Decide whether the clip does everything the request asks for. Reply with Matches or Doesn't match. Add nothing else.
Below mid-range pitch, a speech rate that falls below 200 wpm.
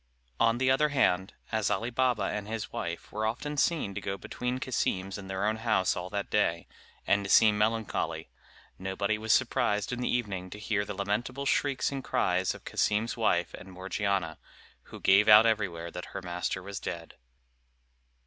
Matches